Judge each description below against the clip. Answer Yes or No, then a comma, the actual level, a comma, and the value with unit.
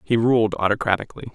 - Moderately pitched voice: No, low, 110 Hz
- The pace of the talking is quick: No, slow, 135 wpm